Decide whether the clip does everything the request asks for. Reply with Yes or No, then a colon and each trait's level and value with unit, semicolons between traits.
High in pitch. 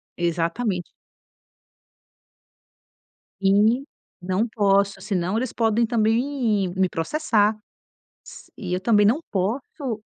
Yes: high, 210 Hz